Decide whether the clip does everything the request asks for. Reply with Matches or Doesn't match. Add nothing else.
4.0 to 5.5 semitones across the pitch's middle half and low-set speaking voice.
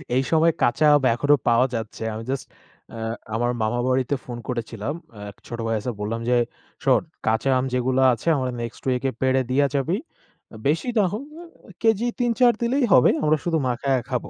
Matches